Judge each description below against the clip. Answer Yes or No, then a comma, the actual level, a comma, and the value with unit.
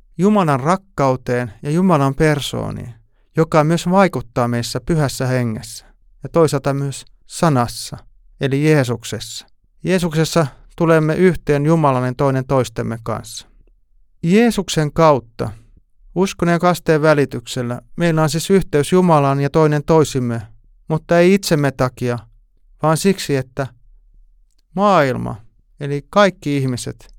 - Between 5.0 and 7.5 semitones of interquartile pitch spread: Yes, average, 5.3 semitones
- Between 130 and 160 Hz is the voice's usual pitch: Yes, medium, 140 Hz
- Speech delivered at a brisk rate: No, average, 110 wpm